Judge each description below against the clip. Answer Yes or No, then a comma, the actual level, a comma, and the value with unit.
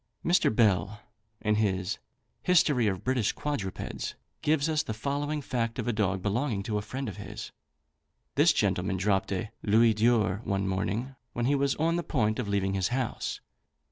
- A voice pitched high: No, low, 110 Hz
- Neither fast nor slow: Yes, average, 175 wpm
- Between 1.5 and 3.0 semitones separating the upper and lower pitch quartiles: No, average, 5.3 semitones